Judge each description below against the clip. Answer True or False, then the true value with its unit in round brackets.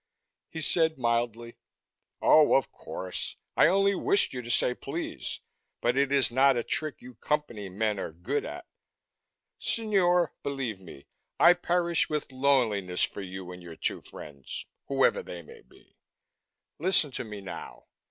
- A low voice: True (125 Hz)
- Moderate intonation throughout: False (7.7 semitones)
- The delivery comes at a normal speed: True (150 wpm)